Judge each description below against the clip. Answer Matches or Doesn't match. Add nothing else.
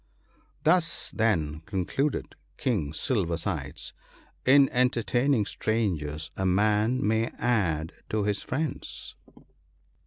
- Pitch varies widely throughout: Matches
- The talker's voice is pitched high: Doesn't match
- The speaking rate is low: Matches